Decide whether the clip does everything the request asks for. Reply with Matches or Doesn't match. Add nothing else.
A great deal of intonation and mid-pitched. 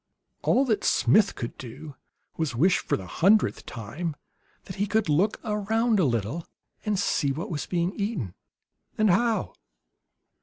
Matches